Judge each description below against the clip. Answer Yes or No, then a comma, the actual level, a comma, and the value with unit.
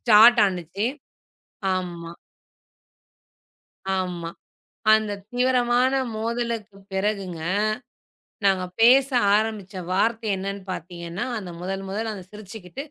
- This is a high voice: Yes, high, 200 Hz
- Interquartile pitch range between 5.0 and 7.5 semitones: No, average, 3.6 semitones